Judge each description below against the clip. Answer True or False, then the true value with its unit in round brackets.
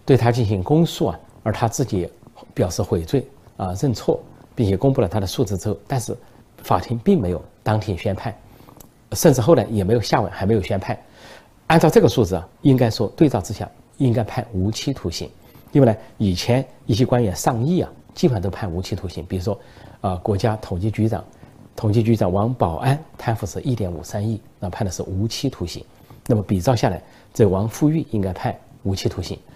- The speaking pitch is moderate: False (110 Hz)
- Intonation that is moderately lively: True (4.2 semitones)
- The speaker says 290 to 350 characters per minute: True (295 characters per minute)